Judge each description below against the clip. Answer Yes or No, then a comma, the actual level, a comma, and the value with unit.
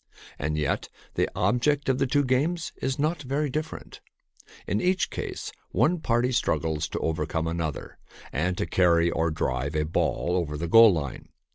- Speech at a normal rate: Yes, average, 170 wpm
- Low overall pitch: Yes, very low, 95 Hz